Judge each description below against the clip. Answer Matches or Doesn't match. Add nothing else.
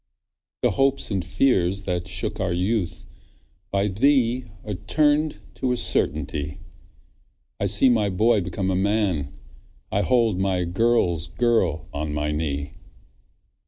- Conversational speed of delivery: Doesn't match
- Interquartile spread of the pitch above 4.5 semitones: Matches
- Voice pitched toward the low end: Matches